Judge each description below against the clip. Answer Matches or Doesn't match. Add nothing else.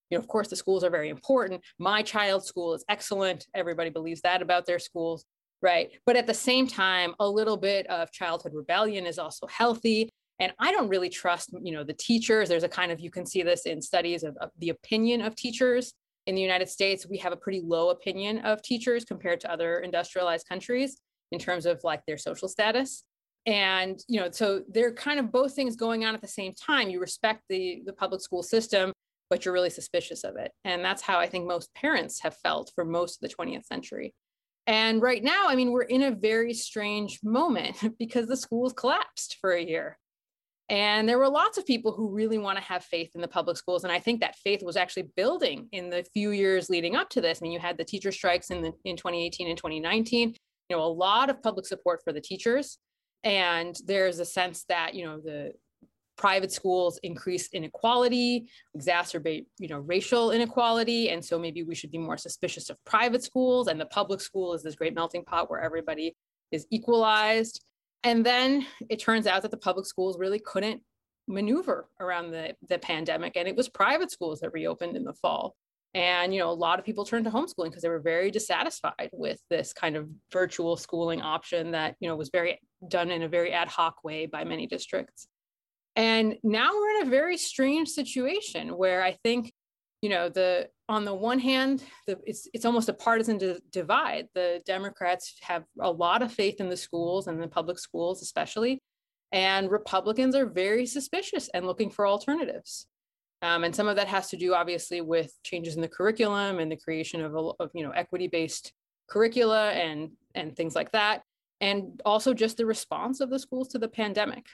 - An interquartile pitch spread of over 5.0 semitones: Doesn't match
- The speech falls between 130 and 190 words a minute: Doesn't match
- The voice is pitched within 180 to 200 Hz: Matches